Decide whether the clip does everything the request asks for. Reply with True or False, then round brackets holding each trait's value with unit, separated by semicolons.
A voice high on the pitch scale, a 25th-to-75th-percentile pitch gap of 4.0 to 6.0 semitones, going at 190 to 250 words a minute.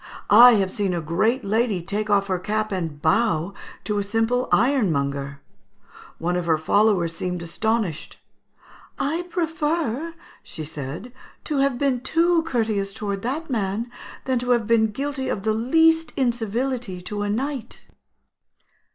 False (220 Hz; 5.5 semitones; 145 wpm)